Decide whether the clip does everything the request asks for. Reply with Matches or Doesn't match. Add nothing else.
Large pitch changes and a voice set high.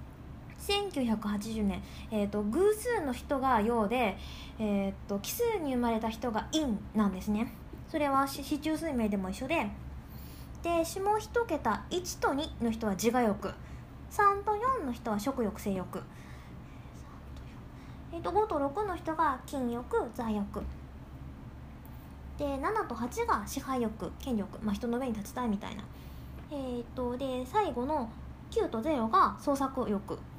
Matches